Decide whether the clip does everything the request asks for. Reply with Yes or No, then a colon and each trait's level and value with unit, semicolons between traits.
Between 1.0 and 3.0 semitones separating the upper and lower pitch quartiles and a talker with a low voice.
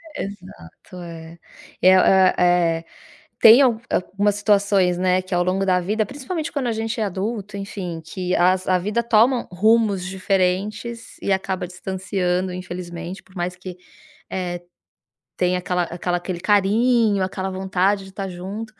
No: narrow, 2.4 semitones; high, 190 Hz